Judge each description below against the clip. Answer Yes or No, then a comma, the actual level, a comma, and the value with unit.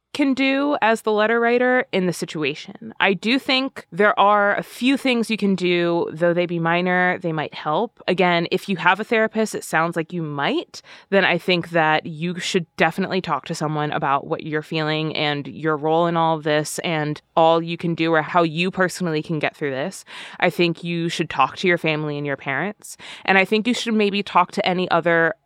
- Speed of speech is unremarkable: No, fast, 220 wpm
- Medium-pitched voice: Yes, medium, 175 Hz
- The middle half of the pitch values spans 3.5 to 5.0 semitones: Yes, average, 4.0 semitones